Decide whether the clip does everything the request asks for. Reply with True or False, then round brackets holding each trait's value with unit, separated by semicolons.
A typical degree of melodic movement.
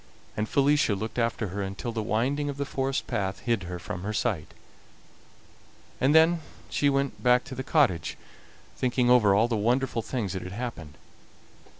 True (5.0 semitones)